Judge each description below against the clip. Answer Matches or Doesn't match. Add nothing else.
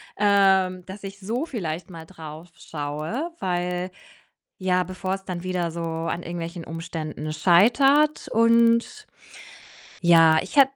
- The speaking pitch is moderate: Matches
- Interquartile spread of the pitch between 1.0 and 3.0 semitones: Doesn't match